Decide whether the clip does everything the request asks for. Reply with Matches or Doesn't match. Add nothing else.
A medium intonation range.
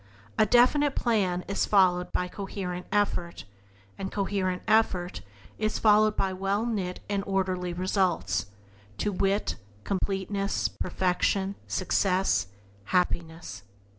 Doesn't match